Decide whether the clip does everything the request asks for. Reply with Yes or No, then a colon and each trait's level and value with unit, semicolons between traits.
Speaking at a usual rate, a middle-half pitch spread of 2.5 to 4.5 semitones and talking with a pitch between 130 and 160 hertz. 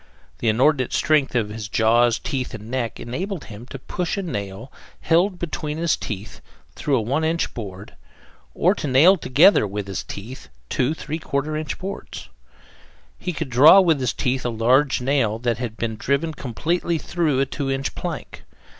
No: average, 170 wpm; wide, 5.5 semitones; low, 135 Hz